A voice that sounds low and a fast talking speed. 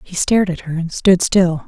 No: medium, 175 Hz; fast, 250 wpm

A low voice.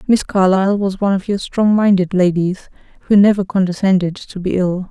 No: high, 190 Hz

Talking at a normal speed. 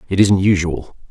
Yes: average, 165 wpm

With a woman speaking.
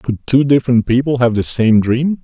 No: male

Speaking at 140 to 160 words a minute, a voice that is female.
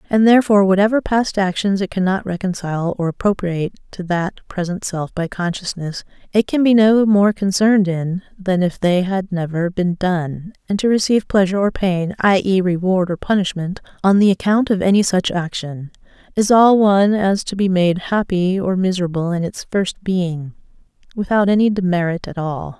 No: average, 175 wpm; female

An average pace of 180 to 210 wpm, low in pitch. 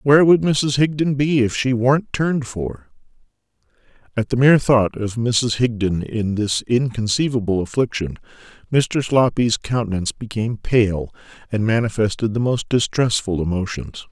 No: slow, 135 wpm; low, 120 Hz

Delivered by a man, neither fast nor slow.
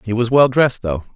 No: male; fast, 260 wpm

